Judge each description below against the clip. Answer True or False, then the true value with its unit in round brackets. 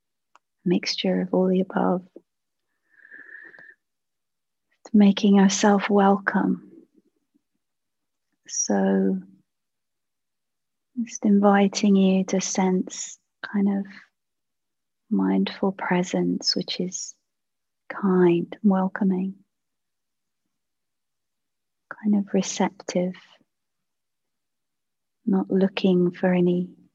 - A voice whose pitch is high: True (195 Hz)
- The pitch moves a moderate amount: False (2.1 semitones)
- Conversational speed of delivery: False (65 wpm)